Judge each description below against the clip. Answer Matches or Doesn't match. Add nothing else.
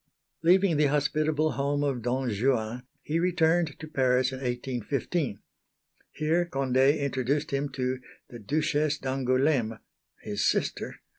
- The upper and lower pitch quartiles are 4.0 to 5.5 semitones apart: Doesn't match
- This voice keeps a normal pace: Doesn't match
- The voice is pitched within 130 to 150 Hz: Matches